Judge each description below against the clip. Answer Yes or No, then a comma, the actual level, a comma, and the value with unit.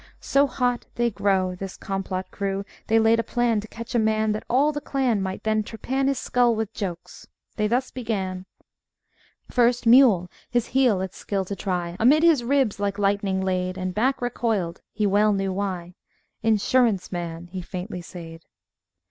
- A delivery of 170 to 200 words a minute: Yes, average, 175 wpm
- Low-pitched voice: No, high, 210 Hz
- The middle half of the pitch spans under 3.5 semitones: No, average, 4.2 semitones